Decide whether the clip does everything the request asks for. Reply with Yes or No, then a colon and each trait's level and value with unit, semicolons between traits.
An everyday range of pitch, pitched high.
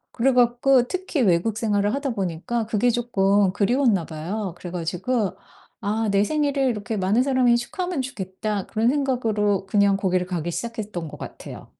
Yes: average, 4.3 semitones; high, 215 Hz